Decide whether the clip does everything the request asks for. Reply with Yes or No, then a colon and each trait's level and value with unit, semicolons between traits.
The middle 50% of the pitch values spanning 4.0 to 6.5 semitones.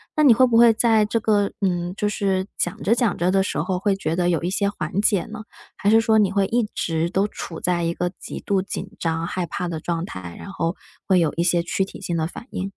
No: average, 3.4 semitones